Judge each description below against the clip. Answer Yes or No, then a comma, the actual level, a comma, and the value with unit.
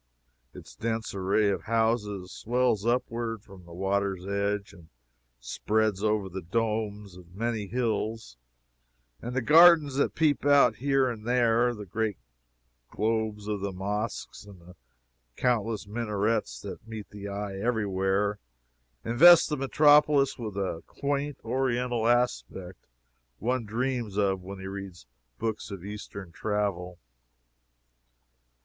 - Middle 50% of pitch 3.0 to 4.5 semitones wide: Yes, average, 3.3 semitones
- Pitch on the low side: Yes, low, 110 Hz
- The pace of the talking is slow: Yes, slow, 130 wpm